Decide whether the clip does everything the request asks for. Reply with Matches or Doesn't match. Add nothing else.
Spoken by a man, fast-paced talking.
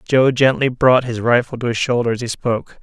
Matches